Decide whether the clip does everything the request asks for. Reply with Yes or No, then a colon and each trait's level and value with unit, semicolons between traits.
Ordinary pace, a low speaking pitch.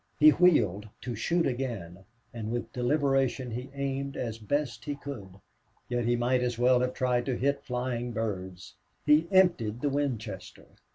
Yes: average, 160 wpm; low, 125 Hz